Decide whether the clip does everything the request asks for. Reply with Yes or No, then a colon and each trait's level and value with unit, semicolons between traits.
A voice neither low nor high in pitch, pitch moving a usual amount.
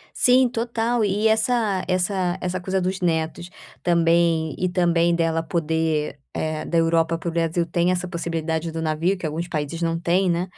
No: medium, 170 Hz; narrow, 2.1 semitones